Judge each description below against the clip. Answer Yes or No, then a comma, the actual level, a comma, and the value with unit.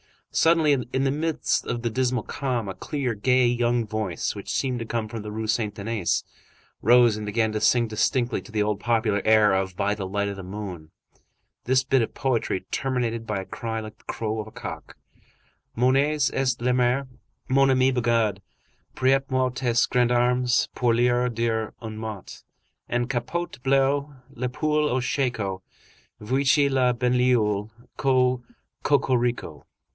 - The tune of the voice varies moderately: Yes, average, 3.1 semitones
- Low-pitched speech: Yes, low, 120 Hz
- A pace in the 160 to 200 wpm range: Yes, average, 165 wpm